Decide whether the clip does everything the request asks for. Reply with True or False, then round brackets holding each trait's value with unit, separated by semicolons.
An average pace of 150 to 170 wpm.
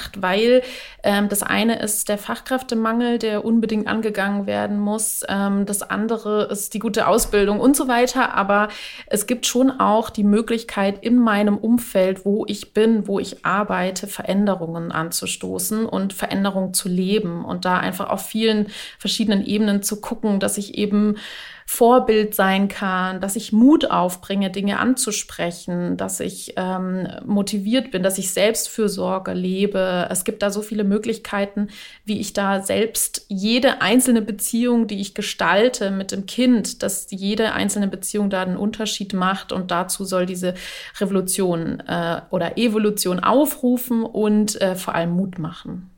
True (155 wpm)